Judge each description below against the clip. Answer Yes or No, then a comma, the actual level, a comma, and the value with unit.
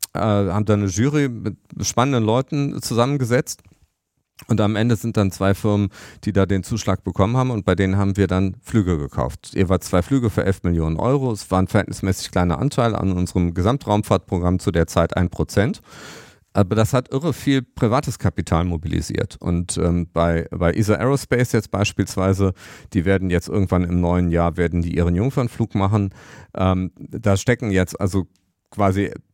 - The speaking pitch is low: Yes, low, 100 Hz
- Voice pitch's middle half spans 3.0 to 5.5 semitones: Yes, average, 4.1 semitones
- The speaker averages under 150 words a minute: No, average, 170 wpm